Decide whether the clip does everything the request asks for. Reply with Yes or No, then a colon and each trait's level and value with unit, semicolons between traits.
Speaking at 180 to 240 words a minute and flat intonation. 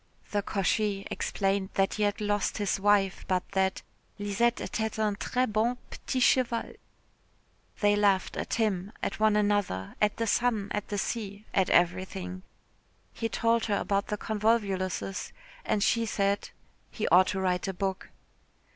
No: average, 155 wpm; narrow, 2.1 semitones